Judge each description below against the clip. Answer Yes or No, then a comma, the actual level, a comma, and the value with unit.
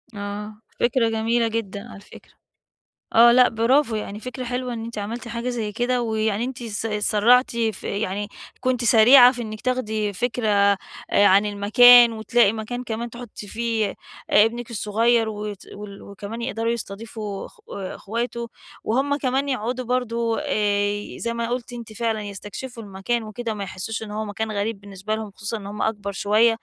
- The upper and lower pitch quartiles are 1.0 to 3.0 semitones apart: Yes, narrow, 2.6 semitones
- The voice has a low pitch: No, high, 225 Hz